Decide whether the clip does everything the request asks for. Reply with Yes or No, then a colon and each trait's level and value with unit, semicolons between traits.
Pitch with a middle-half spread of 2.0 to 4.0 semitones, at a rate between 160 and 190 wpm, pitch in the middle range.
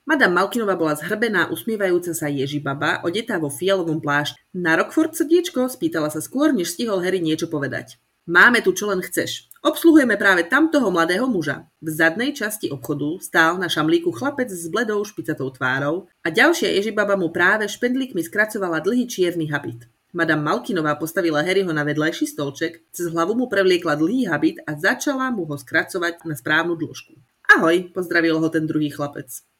No: wide, 5.6 semitones; fast, 165 wpm; medium, 175 Hz